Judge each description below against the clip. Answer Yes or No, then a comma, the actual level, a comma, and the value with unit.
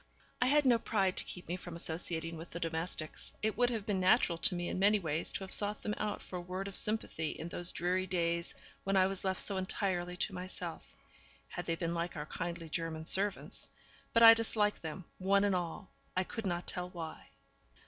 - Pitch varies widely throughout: No, average, 2.9 semitones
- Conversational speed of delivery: No, fast, 215 wpm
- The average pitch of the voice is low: No, medium, 185 Hz